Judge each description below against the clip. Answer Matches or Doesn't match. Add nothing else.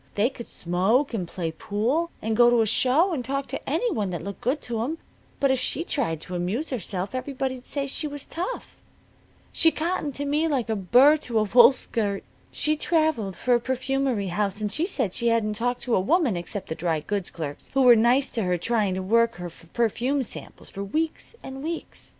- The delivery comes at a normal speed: Doesn't match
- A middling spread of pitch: Doesn't match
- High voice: Matches